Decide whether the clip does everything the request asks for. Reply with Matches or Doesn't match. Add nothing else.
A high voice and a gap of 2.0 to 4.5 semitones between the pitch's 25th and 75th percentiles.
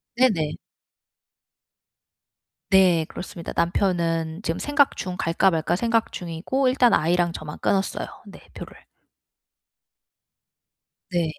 Doesn't match